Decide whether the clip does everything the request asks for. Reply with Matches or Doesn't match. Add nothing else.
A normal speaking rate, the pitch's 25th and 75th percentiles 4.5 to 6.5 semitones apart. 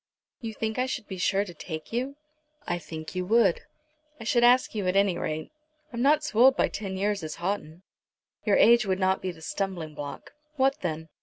Doesn't match